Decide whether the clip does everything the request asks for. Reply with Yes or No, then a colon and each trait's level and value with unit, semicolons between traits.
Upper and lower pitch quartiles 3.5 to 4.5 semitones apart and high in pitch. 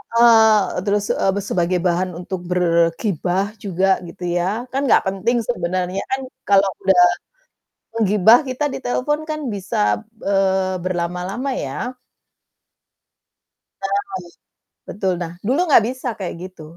Yes: average, 3.8 semitones; high, 195 Hz